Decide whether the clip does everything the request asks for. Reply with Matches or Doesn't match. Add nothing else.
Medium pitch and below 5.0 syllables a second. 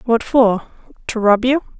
Doesn't match